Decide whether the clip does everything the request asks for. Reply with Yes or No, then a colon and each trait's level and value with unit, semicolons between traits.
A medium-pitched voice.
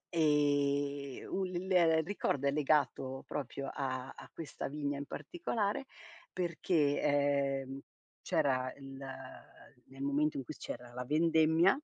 Yes: medium, 145 Hz